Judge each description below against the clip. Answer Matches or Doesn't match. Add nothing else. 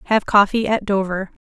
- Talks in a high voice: Matches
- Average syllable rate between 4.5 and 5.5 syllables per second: Matches